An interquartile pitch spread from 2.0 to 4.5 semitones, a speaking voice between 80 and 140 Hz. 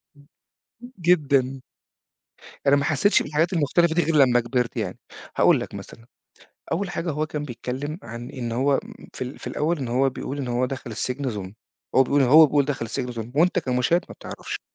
Yes: average, 3.6 semitones; low, 135 Hz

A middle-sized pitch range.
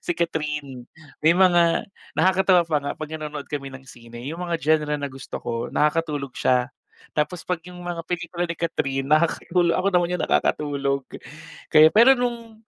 Yes: average, 3.7 semitones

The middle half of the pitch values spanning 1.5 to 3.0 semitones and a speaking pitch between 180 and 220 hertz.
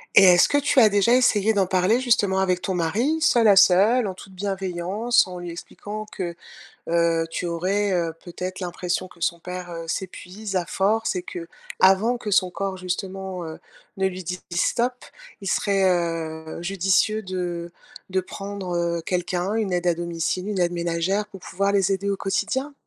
Yes: narrow, 2.4 semitones; medium, 185 Hz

